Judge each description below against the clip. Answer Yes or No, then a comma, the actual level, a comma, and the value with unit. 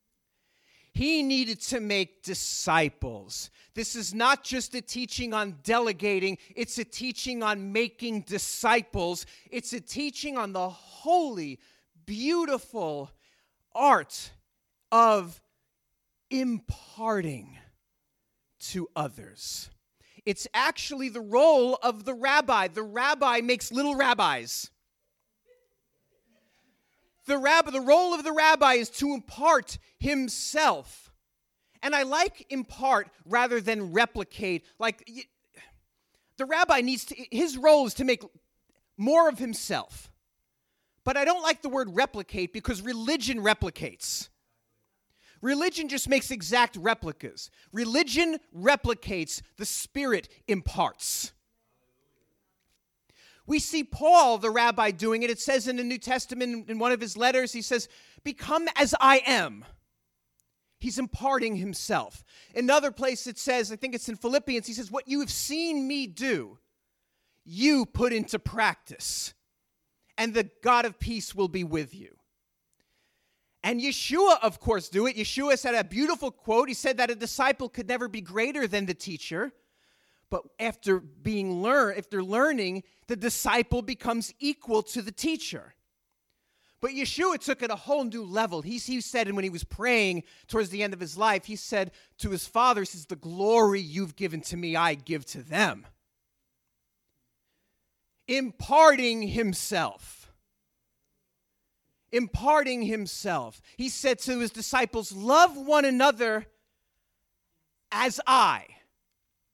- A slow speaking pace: Yes, slow, 130 wpm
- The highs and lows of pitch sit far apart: No, average, 4.8 semitones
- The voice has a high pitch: Yes, high, 235 Hz